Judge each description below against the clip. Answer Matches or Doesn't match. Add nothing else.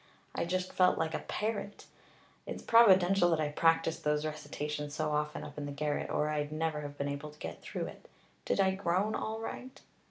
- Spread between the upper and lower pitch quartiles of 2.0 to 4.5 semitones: Matches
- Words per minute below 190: Doesn't match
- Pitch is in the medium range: Matches